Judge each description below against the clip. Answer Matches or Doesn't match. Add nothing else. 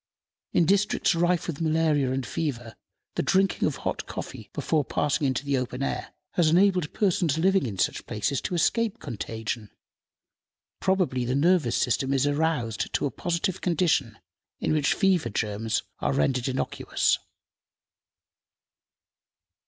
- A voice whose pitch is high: Doesn't match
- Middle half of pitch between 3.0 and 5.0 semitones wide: Doesn't match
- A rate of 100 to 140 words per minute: Matches